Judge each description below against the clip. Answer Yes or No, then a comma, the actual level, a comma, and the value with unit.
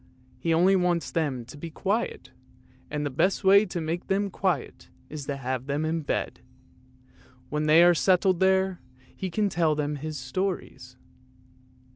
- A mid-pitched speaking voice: Yes, medium, 165 Hz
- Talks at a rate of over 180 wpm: No, average, 160 wpm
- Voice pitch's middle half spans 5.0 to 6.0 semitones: No, average, 4.1 semitones